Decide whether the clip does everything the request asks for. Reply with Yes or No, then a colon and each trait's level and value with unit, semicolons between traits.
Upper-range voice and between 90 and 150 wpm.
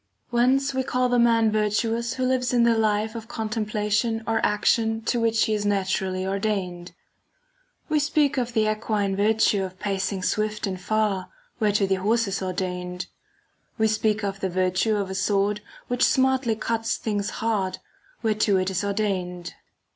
No: high, 215 Hz; average, 170 wpm